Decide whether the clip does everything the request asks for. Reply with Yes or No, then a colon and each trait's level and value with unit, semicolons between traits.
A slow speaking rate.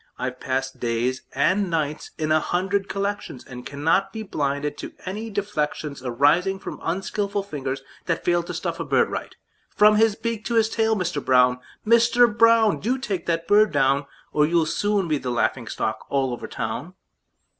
No: average, 175 wpm